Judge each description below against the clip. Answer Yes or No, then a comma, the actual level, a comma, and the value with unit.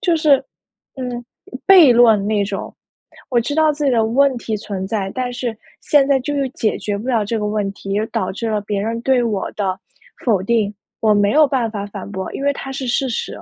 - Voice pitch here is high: Yes, high, 230 Hz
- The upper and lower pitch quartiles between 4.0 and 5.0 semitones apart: Yes, average, 4.5 semitones